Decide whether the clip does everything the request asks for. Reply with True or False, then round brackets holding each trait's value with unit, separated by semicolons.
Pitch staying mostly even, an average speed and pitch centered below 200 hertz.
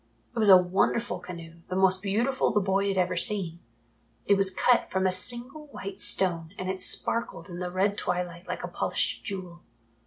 True (2.2 semitones; 190 wpm; 190 Hz)